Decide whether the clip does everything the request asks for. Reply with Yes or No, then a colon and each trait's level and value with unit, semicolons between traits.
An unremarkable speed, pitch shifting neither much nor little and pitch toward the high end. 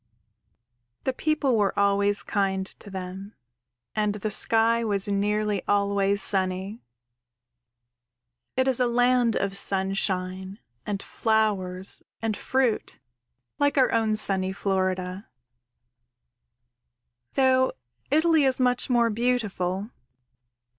No: slow, 105 wpm; average, 3.8 semitones; high, 205 Hz